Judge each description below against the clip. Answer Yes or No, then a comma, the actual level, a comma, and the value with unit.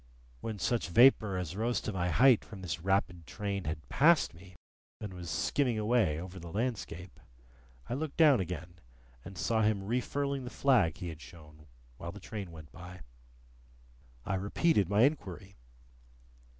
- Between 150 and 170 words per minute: Yes, average, 160 wpm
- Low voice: Yes, very low, 95 Hz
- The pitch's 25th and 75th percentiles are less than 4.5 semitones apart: No, average, 5.3 semitones